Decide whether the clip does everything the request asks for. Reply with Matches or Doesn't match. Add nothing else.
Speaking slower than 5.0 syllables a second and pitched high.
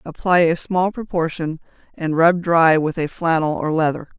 Doesn't match